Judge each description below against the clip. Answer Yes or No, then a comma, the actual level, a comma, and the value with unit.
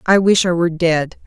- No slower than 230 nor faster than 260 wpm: Yes, fast, 235 wpm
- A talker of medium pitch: Yes, medium, 175 Hz